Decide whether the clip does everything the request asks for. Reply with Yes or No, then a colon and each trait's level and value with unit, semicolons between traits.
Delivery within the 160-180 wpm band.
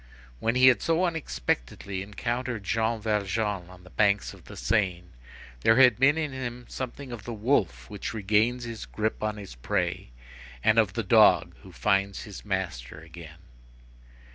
Yes: average, 165 wpm